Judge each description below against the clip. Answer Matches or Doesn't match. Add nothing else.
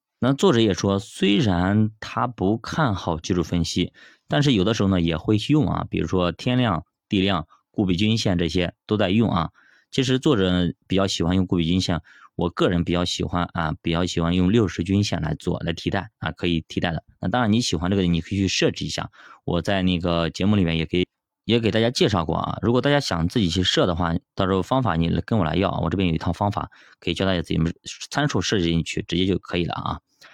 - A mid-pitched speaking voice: Doesn't match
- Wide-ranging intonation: Doesn't match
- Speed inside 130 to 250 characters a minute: Doesn't match